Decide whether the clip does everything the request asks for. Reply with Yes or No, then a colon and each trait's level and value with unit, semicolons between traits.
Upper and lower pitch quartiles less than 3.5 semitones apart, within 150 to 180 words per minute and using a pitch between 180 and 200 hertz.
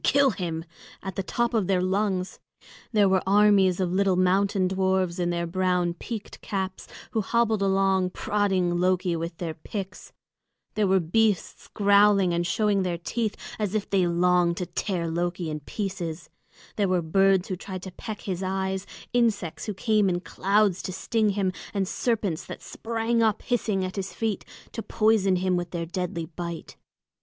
Yes: narrow, 2.5 semitones; average, 170 wpm; high, 190 Hz